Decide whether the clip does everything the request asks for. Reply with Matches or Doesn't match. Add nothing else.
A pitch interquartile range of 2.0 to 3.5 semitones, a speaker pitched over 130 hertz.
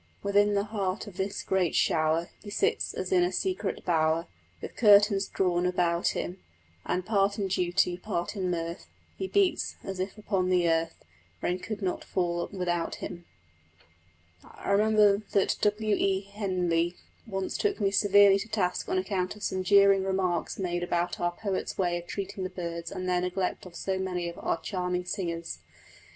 Matches